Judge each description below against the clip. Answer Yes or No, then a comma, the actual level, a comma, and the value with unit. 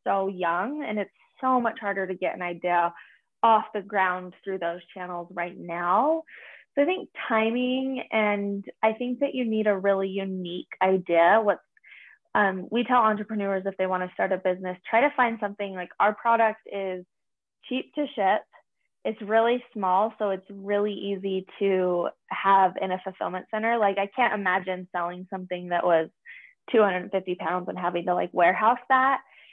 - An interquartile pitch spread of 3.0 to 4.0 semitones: Yes, average, 3.4 semitones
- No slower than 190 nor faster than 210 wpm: No, average, 175 wpm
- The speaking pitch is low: No, high, 195 Hz